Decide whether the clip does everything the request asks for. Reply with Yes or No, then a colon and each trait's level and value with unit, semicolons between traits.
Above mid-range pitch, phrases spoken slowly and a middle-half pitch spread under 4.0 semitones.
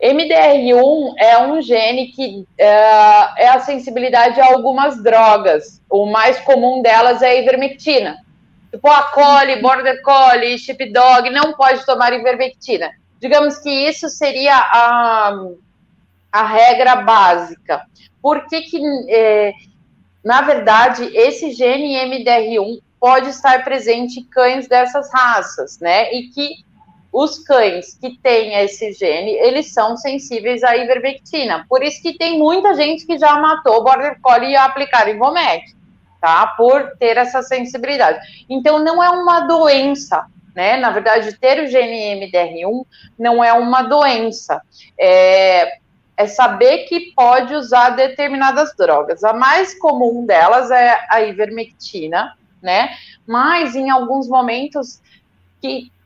No: very high, 255 Hz; average, 130 wpm; average, 3.6 semitones